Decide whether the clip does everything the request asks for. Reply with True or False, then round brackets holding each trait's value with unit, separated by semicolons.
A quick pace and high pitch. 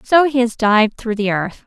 True (250 wpm; 230 Hz)